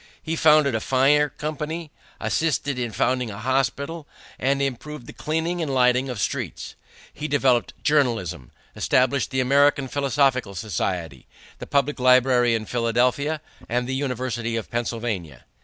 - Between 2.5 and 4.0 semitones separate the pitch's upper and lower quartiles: Yes, average, 3.4 semitones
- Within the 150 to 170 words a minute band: No, average, 140 wpm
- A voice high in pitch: No, low, 130 Hz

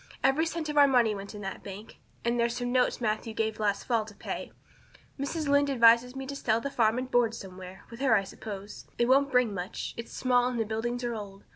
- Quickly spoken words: Yes, fast, 235 wpm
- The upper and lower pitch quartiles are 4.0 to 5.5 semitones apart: No, average, 3.3 semitones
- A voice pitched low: No, high, 235 Hz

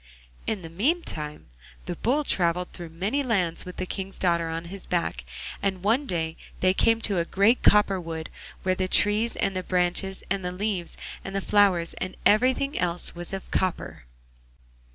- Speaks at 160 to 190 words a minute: Yes, average, 175 wpm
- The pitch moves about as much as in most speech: Yes, average, 3.2 semitones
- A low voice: No, medium, 185 Hz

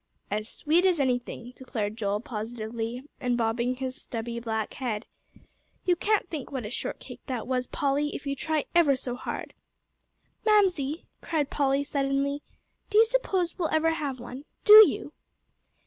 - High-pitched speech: Yes, very high, 270 Hz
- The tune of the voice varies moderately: Yes, average, 4.8 semitones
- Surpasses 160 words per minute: No, average, 155 wpm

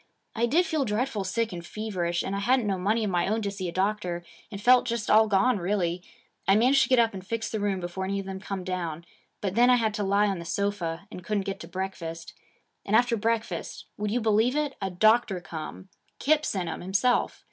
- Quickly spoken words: Yes, fast, 235 wpm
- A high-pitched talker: Yes, high, 200 Hz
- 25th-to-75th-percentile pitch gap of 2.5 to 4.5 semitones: Yes, average, 3.7 semitones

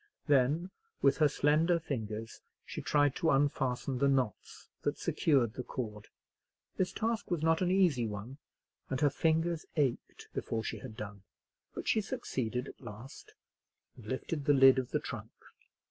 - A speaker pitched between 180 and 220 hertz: No, low, 135 Hz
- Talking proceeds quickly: No, average, 160 wpm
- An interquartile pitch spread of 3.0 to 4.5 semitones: No, average, 4.9 semitones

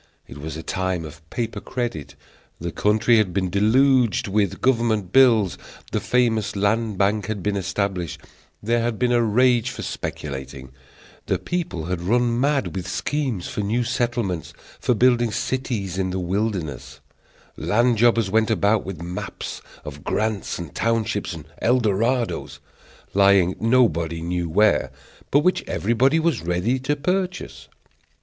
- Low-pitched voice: Yes, low, 105 Hz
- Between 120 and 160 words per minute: Yes, average, 145 wpm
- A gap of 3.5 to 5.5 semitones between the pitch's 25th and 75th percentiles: Yes, average, 4.9 semitones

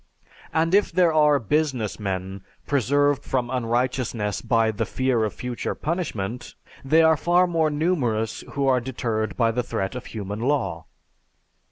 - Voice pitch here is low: Yes, low, 125 Hz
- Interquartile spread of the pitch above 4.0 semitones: Yes, average, 5.1 semitones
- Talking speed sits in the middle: Yes, average, 150 wpm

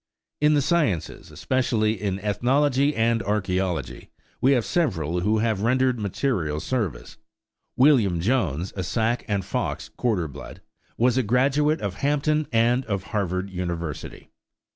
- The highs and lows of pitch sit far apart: Yes, wide, 5.8 semitones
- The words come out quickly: No, slow, 135 wpm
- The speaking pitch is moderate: No, low, 110 Hz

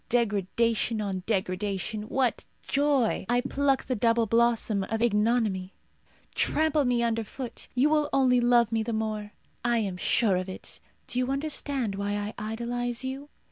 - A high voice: Yes, high, 230 Hz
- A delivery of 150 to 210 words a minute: Yes, average, 155 wpm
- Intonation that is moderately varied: Yes, average, 3.2 semitones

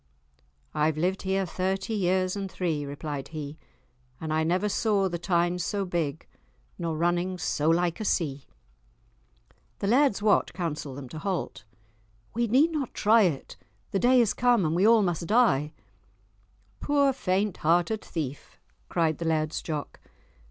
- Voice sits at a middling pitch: Yes, medium, 180 Hz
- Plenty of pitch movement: No, average, 4.6 semitones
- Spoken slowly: No, average, 150 wpm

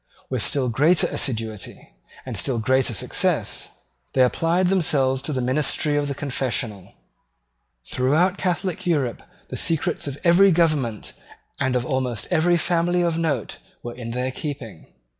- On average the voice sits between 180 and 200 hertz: No, medium, 140 Hz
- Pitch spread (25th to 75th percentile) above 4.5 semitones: Yes, average, 4.9 semitones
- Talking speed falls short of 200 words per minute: Yes, average, 140 wpm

